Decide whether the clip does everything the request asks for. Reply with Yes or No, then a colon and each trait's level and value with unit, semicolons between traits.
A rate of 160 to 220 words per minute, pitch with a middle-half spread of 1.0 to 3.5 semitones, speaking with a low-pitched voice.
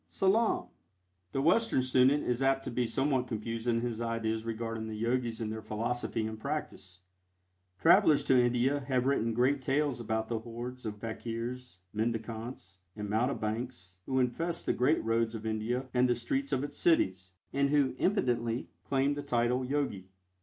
Yes: average, 165 wpm; average, 3.1 semitones; low, 120 Hz